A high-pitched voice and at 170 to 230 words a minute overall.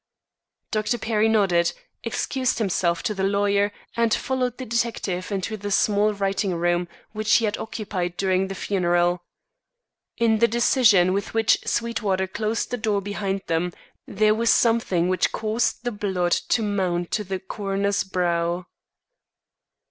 No: high, 200 Hz; average, 145 wpm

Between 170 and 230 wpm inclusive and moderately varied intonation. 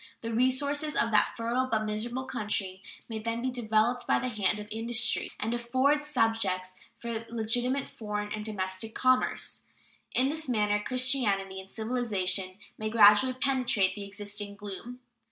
No: average, 150 wpm; average, 3.3 semitones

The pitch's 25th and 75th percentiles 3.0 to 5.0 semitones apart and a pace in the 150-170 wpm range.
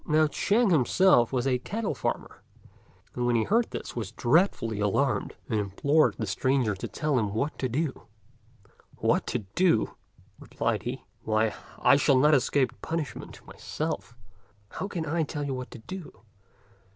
No: wide, 5.6 semitones; average, 160 wpm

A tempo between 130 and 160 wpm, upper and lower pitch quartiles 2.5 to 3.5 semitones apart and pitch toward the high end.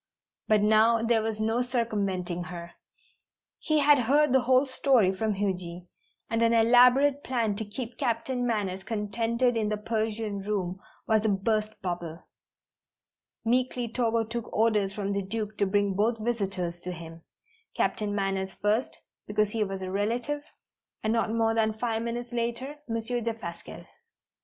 Yes: average, 150 wpm; average, 2.9 semitones; high, 220 Hz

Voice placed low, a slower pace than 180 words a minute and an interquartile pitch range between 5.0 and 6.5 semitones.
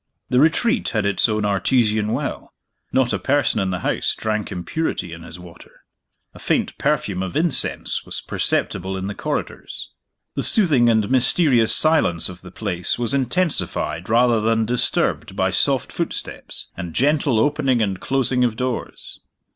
Yes: low, 115 Hz; average, 155 wpm; wide, 5.5 semitones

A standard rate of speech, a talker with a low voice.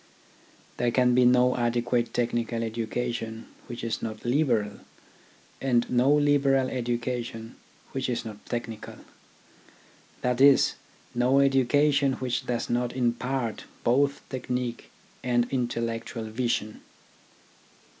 No: slow, 105 wpm; low, 120 Hz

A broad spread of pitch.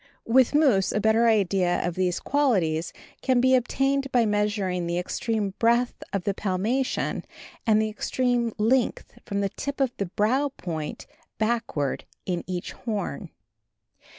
No: average, 4.8 semitones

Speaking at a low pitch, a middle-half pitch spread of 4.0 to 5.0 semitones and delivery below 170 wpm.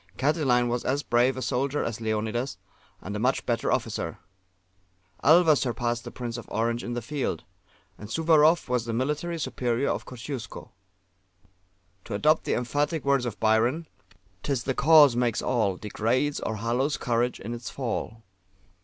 No: low, 125 Hz; average, 3.4 semitones; average, 155 wpm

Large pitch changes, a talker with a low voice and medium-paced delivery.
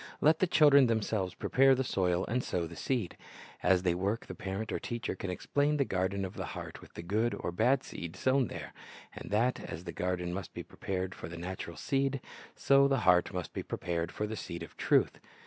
No: wide, 6.5 semitones; low, 100 Hz; fast, 215 wpm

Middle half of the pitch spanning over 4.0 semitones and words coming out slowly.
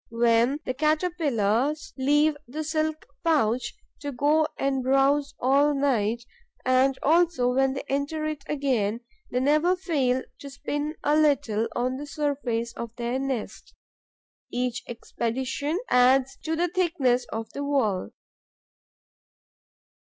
No: average, 3.5 semitones; slow, 125 wpm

